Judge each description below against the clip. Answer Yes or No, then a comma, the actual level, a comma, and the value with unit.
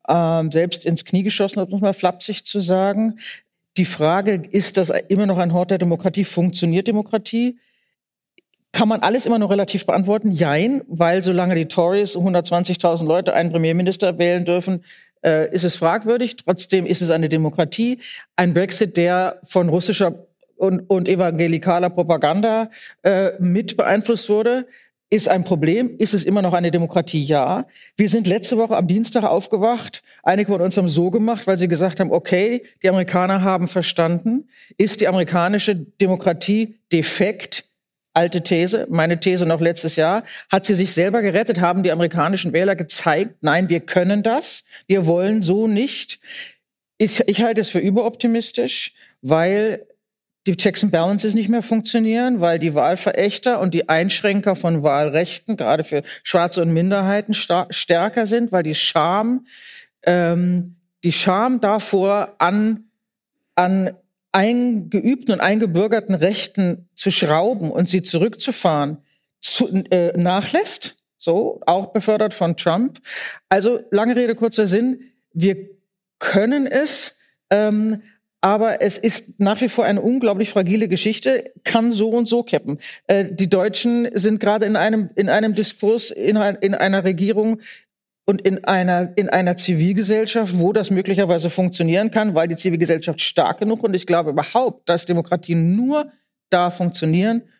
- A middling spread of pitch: Yes, average, 3.7 semitones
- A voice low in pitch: No, high, 195 Hz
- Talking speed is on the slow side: No, average, 150 wpm